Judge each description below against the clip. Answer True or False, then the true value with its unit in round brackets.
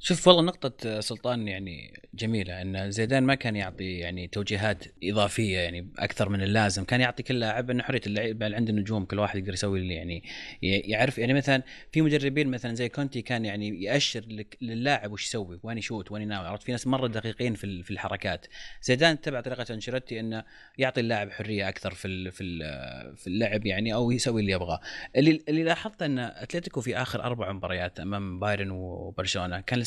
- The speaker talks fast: True (185 wpm)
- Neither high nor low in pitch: False (110 Hz)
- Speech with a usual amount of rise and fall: True (4.1 semitones)